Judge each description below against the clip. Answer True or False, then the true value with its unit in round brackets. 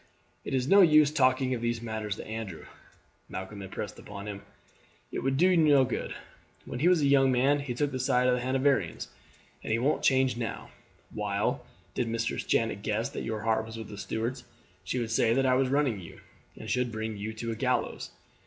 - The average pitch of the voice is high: False (120 Hz)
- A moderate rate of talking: False (210 wpm)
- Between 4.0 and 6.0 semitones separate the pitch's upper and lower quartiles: False (3.4 semitones)